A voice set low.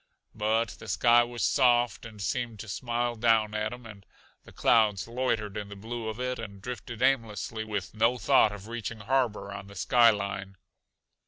Yes: low, 110 Hz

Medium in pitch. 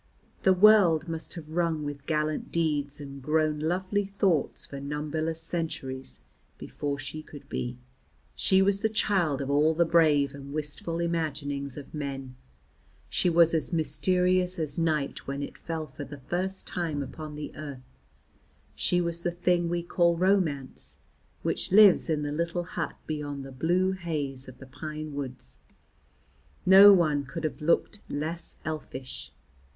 Yes: medium, 155 Hz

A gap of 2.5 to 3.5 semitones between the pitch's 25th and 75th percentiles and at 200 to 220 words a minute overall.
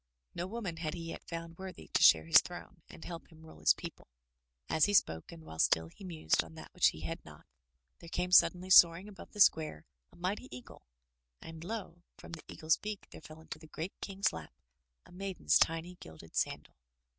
Yes: average, 2.9 semitones; fast, 205 wpm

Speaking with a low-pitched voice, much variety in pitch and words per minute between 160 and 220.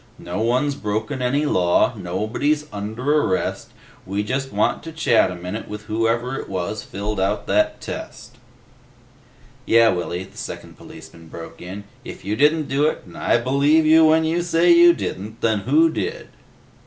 Yes: low, 115 Hz; wide, 6.6 semitones; average, 165 wpm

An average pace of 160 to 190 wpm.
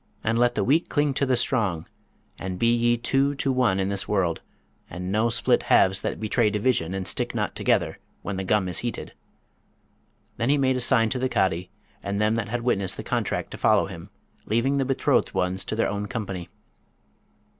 No: average, 200 wpm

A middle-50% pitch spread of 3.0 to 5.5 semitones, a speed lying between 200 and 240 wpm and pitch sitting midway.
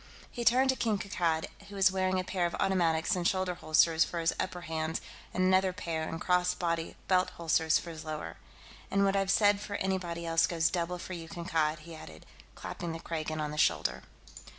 No: narrow, 2.6 semitones; fast, 205 wpm; medium, 175 Hz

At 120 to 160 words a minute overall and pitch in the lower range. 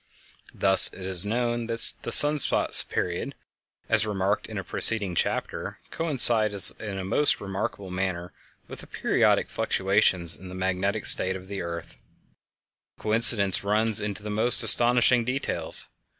Yes: average, 150 wpm; low, 100 Hz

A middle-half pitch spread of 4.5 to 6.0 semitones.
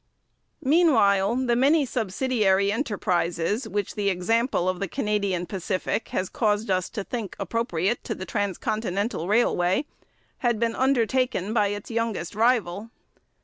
No: average, 3.7 semitones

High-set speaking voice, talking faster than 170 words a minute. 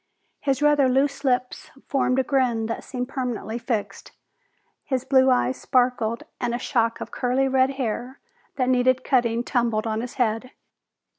No: very high, 250 Hz; average, 155 wpm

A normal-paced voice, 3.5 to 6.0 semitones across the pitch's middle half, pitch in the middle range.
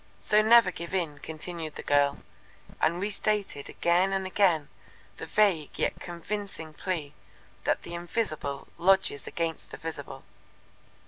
No: slow, 130 wpm; average, 3.9 semitones; medium, 170 Hz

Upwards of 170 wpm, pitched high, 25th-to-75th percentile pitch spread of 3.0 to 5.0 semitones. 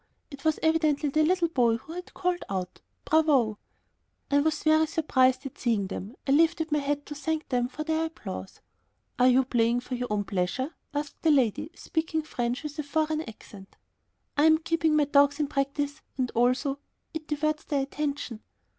Yes: average, 180 wpm; very high, 290 Hz; average, 3.8 semitones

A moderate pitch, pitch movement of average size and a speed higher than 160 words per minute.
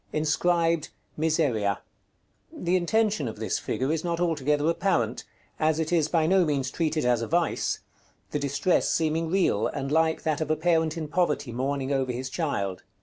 Yes: medium, 155 Hz; average, 3.6 semitones; average, 170 wpm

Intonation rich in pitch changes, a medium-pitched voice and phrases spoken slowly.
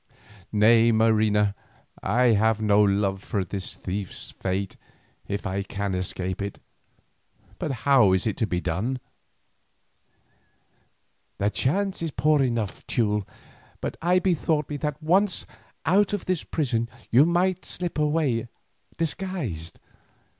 No: wide, 7.4 semitones; low, 115 Hz; slow, 125 wpm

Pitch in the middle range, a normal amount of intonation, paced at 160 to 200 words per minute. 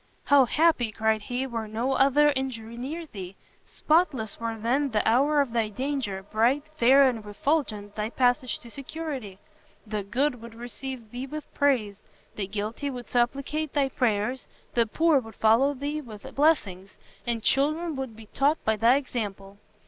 No: high, 245 Hz; average, 4.3 semitones; average, 165 wpm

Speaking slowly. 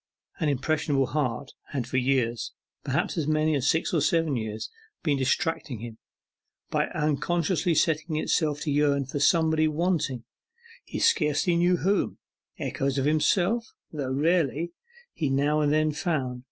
No: average, 145 wpm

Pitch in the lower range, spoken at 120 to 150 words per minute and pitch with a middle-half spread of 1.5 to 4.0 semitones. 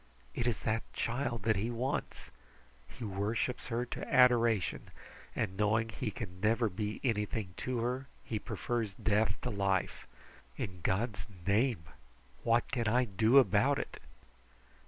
Yes: low, 110 Hz; average, 140 wpm; average, 2.8 semitones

